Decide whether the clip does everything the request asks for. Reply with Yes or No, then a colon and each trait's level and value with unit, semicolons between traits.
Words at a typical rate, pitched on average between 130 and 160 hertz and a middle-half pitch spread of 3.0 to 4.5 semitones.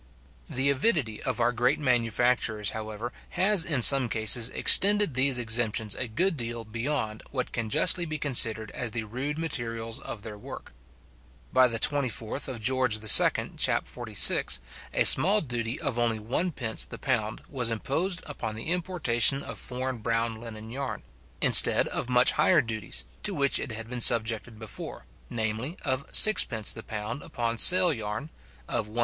No: average, 160 wpm; low, 120 Hz; average, 3.9 semitones